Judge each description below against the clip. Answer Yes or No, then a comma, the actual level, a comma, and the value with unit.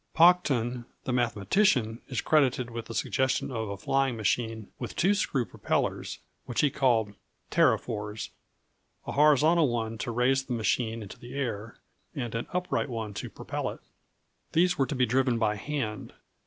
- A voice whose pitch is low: Yes, low, 120 Hz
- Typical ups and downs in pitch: Yes, average, 3.5 semitones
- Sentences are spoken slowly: No, average, 160 wpm